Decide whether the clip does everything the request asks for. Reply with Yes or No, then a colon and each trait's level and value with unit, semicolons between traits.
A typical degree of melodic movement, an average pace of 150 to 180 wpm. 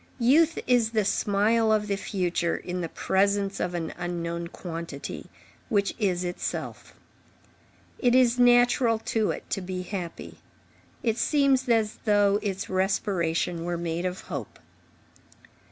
No: average, 4.4 semitones; slow, 135 wpm